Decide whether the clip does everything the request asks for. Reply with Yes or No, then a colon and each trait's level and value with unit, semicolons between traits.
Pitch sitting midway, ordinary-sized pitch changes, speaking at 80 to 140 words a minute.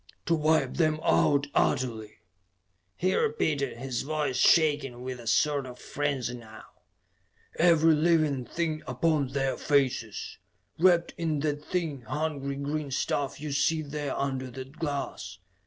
Yes: medium, 145 Hz; average, 3.2 semitones; slow, 135 wpm